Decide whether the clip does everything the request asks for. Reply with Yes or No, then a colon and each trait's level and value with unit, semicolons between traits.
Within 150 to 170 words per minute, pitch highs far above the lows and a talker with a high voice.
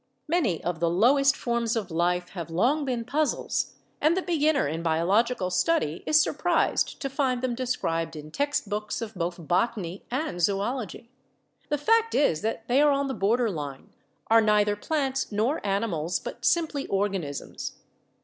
Yes: average, 160 wpm; wide, 7.7 semitones; high, 225 Hz